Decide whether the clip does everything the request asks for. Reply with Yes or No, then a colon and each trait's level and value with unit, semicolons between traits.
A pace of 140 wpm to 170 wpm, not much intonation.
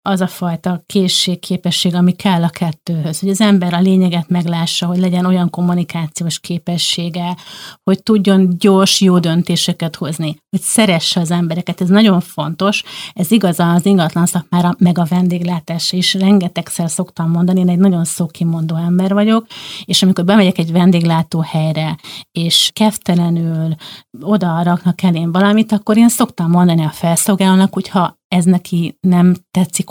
Yes: average, 150 wpm; narrow, 2.0 semitones